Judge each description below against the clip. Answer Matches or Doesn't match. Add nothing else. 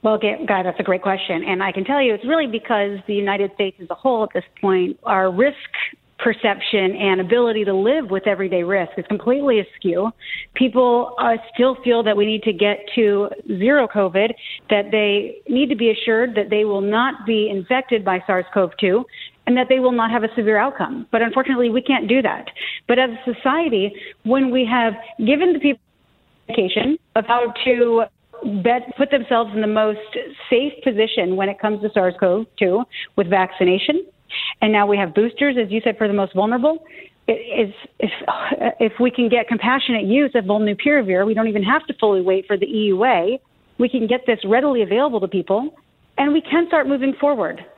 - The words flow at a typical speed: Matches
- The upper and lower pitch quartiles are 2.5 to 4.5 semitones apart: Matches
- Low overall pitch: Doesn't match